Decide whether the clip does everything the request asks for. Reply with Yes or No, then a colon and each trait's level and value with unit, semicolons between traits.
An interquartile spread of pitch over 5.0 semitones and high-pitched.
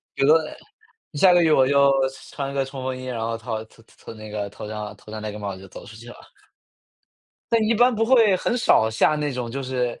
No: wide, 5.4 semitones; low, 130 Hz